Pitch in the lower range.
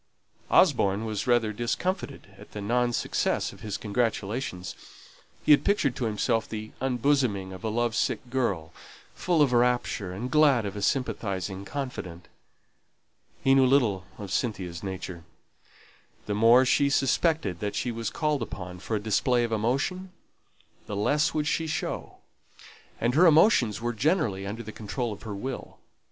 Yes: low, 115 Hz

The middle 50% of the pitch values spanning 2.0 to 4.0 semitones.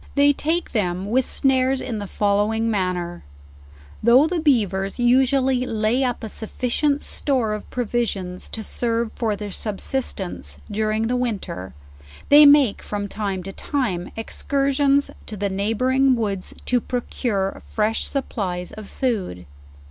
No: average, 4.5 semitones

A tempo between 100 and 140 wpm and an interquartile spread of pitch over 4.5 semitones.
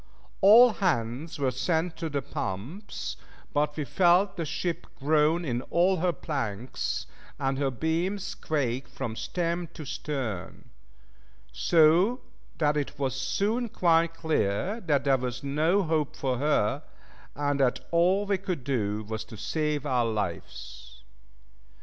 Yes: slow, 135 wpm; average, 5.1 semitones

